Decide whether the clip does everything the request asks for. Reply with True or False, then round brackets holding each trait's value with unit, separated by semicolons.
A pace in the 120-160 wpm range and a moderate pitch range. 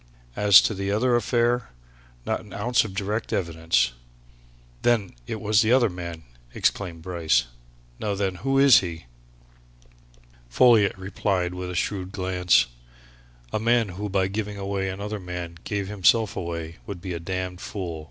True (150 wpm; 3.2 semitones)